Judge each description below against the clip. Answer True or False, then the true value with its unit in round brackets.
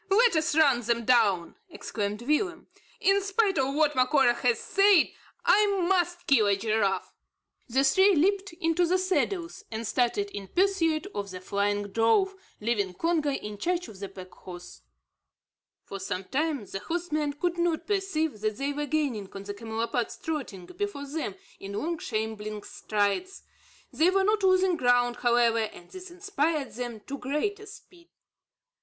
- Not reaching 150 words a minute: False (160 wpm)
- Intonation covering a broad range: True (8.5 semitones)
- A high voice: True (280 Hz)